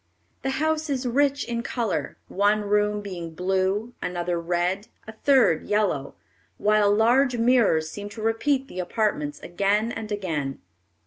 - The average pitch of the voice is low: No, high, 210 Hz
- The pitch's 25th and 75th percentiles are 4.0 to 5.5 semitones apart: Yes, average, 4.7 semitones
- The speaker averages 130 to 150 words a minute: Yes, average, 140 wpm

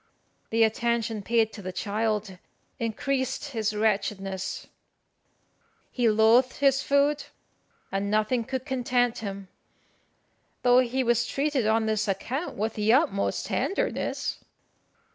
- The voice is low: No, high, 225 Hz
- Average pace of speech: No, slow, 115 wpm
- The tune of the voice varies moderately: Yes, average, 3.4 semitones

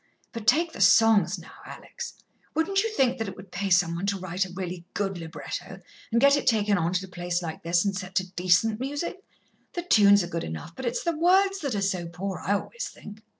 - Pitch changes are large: Yes, wide, 6.0 semitones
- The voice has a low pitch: No, high, 200 Hz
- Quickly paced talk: Yes, fast, 230 wpm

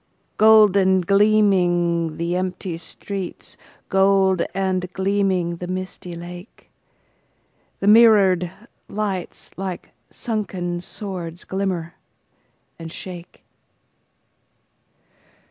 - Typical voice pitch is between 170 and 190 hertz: Yes, medium, 185 Hz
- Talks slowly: Yes, slow, 70 wpm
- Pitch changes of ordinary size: No, narrow, 2.1 semitones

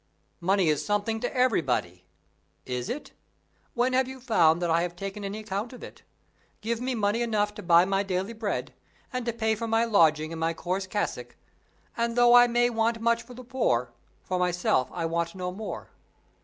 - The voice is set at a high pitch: Yes, high, 205 Hz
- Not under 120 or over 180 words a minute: No, average, 195 wpm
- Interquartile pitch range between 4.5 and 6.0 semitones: Yes, average, 5.1 semitones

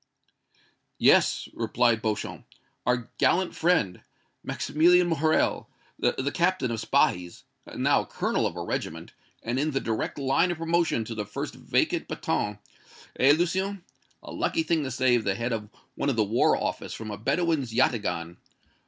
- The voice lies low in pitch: Yes, low, 130 Hz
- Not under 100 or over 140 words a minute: No, average, 155 wpm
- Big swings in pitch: Yes, wide, 7.0 semitones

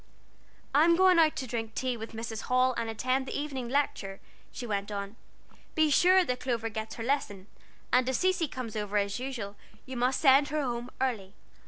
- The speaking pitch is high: Yes, very high, 250 Hz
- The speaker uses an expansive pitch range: No, average, 3.7 semitones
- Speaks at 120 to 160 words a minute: No, average, 190 wpm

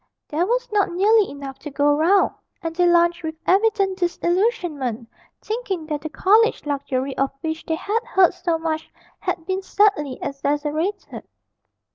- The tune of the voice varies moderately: Yes, average, 4.8 semitones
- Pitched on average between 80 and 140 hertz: No, very high, 345 Hz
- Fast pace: No, average, 150 wpm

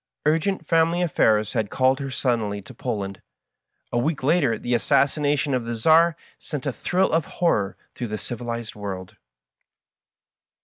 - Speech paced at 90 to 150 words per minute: Yes, average, 145 wpm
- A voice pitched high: No, low, 130 Hz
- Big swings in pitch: Yes, wide, 6.2 semitones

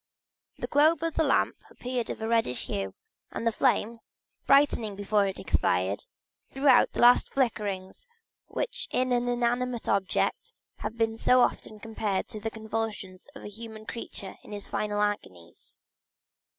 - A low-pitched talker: No, high, 225 Hz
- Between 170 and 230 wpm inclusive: No, average, 155 wpm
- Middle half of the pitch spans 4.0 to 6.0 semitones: No, average, 3.3 semitones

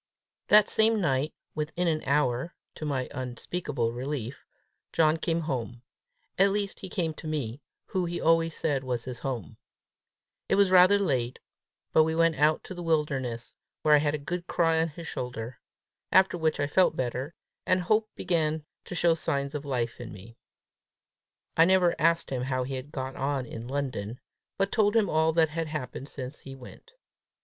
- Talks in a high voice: No, medium, 150 Hz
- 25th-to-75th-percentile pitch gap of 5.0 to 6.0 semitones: No, average, 4.5 semitones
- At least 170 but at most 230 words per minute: Yes, average, 180 wpm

